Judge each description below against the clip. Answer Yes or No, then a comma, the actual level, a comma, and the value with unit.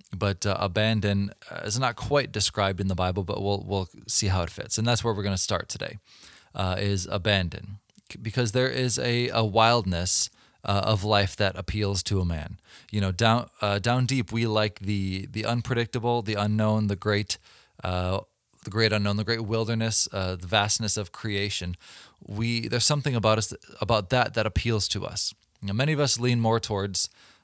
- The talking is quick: No, average, 190 wpm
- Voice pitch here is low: Yes, low, 105 Hz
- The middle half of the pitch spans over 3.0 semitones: No, average, 2.7 semitones